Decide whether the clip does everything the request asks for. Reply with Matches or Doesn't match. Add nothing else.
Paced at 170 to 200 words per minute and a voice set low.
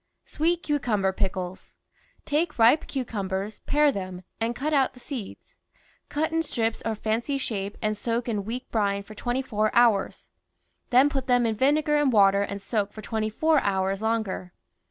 Doesn't match